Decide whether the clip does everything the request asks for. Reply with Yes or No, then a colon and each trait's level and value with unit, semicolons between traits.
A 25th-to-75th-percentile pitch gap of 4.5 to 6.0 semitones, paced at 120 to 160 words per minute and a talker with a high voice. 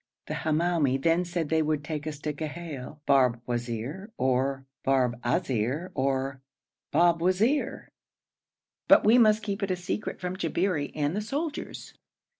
No: average, 5.3 semitones; slow, 135 wpm; medium, 155 Hz